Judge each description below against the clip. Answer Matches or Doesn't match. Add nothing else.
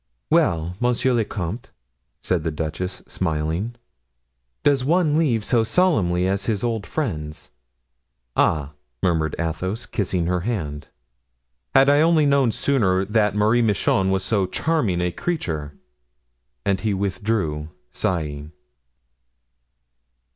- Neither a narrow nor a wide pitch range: Doesn't match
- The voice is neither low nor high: Doesn't match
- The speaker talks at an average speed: Doesn't match